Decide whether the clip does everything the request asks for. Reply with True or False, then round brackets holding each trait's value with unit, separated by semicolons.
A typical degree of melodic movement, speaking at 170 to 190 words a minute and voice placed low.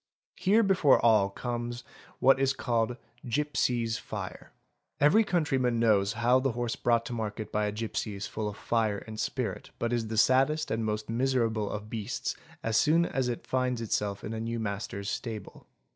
True (3.1 semitones; 180 wpm; 115 Hz)